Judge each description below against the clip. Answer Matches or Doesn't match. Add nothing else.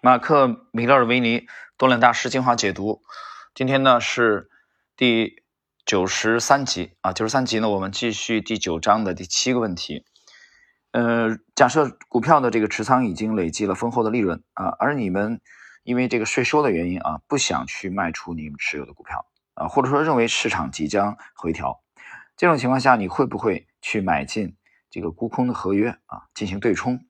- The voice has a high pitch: Doesn't match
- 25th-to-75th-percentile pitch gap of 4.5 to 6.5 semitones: Doesn't match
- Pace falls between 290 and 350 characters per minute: Doesn't match